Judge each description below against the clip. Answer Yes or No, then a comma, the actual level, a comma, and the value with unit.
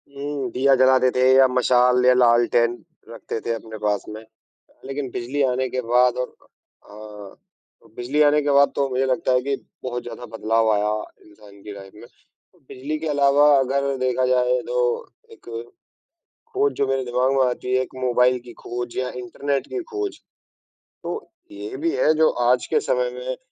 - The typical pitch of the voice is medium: No, low, 125 Hz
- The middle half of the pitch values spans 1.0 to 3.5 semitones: Yes, narrow, 2.6 semitones